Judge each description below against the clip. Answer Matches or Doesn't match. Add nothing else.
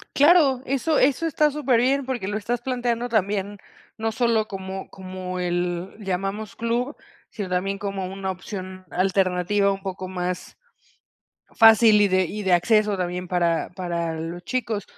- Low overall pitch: Doesn't match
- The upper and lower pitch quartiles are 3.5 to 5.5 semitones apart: Matches